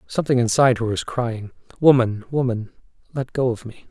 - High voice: No, low, 120 Hz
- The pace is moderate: Yes, average, 170 wpm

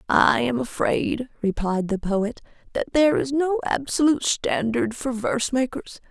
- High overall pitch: Yes, high, 245 Hz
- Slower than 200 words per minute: Yes, average, 145 wpm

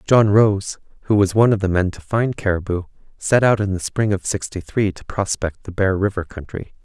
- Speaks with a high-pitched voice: No, low, 100 Hz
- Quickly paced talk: Yes, fast, 220 wpm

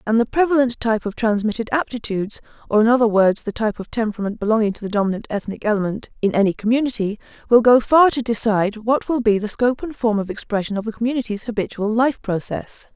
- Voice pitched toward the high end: Yes, high, 225 Hz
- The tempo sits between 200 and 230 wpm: Yes, fast, 205 wpm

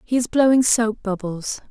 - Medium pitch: No, high, 225 Hz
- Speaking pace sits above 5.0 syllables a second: No, 4.6 syllables/s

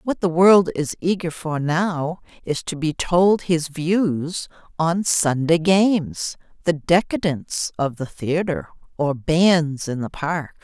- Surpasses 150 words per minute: No, average, 145 wpm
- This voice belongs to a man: No, female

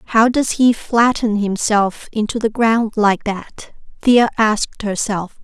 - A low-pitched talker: No, high, 220 Hz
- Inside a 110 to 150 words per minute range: Yes, average, 145 wpm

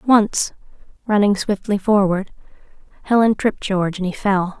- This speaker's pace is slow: Yes, slow, 130 wpm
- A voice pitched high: Yes, high, 200 Hz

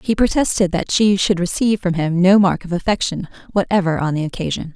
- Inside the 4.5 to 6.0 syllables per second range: Yes, 5.9 syllables/s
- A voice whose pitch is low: No, medium, 185 Hz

